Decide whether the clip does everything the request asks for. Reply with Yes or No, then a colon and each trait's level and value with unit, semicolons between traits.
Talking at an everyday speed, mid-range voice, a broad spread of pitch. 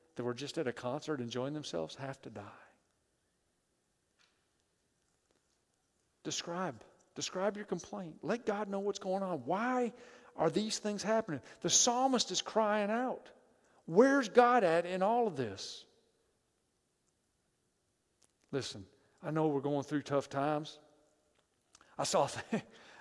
No: slow, 130 wpm; medium, 165 Hz; wide, 6.9 semitones